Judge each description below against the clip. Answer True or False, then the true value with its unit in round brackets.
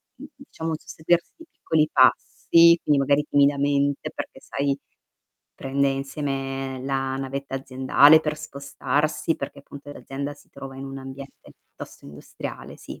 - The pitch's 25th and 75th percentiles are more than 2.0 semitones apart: False (1.6 semitones)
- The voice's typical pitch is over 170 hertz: False (140 Hz)